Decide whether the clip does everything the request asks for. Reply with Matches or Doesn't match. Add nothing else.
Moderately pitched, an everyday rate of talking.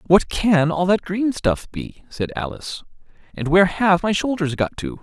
Matches